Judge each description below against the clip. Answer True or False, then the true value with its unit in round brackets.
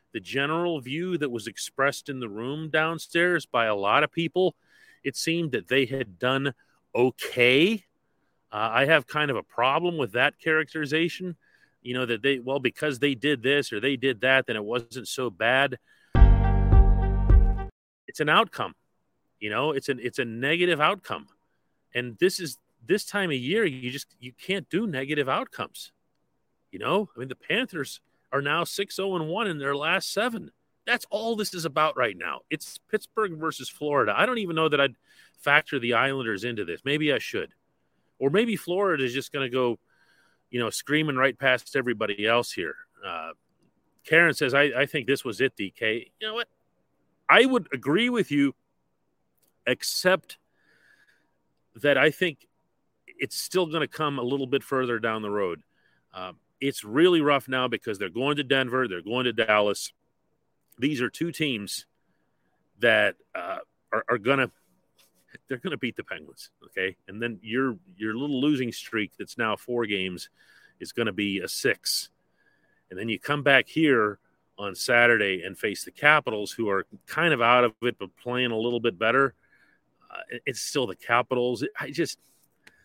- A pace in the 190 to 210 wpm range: False (175 wpm)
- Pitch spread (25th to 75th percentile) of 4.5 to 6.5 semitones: True (5.0 semitones)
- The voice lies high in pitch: False (135 Hz)